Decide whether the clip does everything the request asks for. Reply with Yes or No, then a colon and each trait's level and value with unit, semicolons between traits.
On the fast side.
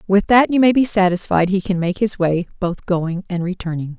Yes: fast, 225 wpm